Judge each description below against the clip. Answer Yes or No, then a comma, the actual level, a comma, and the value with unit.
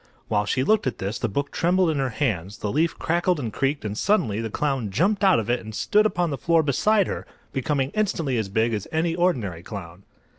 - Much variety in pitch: Yes, wide, 7.9 semitones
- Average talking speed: No, fast, 225 wpm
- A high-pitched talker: No, low, 135 Hz